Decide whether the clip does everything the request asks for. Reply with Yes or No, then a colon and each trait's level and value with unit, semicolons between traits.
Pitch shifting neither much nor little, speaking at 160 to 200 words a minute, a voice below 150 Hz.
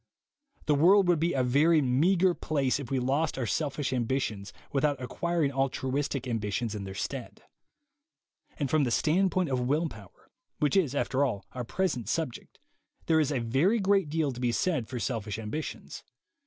Yes: average, 4.6 semitones; average, 170 wpm; medium, 140 Hz